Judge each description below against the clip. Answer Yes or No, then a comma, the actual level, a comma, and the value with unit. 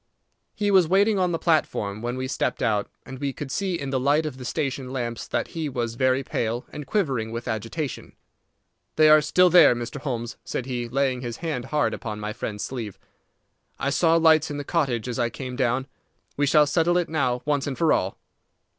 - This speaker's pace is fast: Yes, fast, 210 wpm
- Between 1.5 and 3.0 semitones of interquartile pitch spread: No, average, 4.5 semitones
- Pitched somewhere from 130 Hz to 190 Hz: Yes, low, 135 Hz